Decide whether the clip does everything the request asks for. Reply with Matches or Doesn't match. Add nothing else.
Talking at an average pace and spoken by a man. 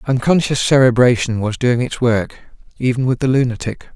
Matches